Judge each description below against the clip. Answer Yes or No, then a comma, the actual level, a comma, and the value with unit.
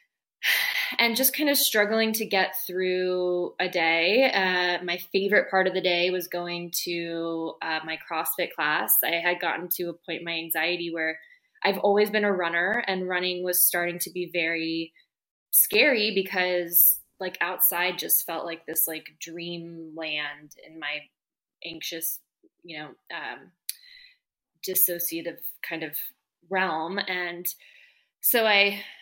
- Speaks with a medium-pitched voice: Yes, medium, 180 Hz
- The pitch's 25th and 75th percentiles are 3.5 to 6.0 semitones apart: No, average, 3.1 semitones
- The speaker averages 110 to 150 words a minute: Yes, average, 145 wpm